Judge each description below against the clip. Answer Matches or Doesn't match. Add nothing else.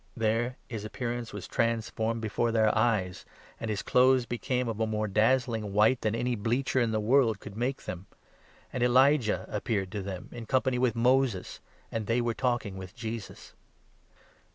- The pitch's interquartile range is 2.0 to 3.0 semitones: Matches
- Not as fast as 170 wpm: Doesn't match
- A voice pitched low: Matches